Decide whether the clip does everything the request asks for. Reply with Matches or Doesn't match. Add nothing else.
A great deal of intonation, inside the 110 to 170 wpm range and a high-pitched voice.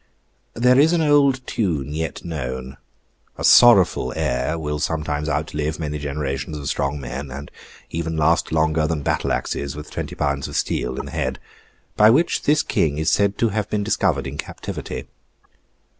Doesn't match